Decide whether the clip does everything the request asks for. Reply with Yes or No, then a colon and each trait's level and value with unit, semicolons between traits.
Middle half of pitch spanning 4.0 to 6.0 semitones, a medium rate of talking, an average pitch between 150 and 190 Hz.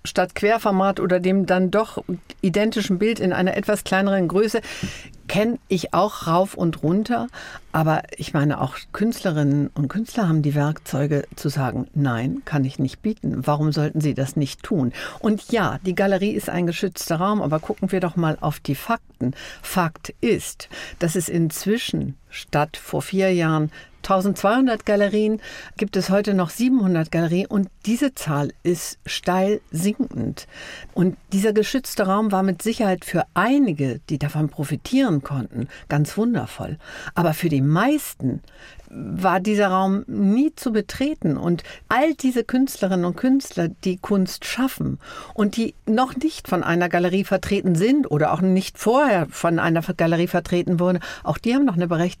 Yes: average, 5.2 semitones; average, 160 wpm; medium, 185 Hz